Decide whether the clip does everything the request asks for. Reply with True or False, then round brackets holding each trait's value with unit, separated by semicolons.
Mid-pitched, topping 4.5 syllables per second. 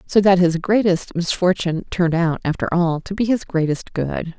True (175 Hz; 5.1 syllables/s)